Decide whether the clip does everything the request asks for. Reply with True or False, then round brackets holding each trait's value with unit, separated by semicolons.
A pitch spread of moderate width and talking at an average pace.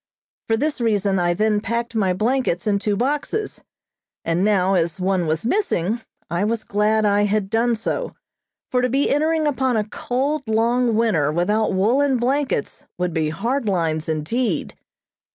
True (5.0 semitones; 160 wpm)